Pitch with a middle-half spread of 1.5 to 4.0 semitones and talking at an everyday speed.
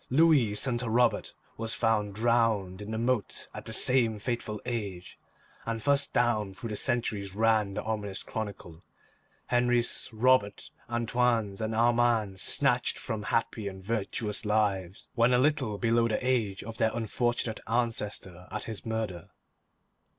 Yes: narrow, 2.6 semitones; average, 145 wpm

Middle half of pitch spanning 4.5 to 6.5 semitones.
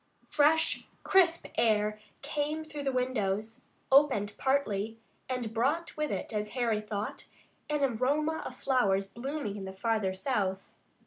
Yes: wide, 5.6 semitones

